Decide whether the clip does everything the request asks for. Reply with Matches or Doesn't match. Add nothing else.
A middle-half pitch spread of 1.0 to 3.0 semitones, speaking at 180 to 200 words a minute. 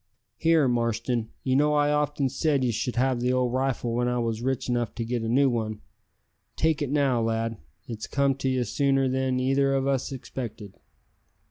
Matches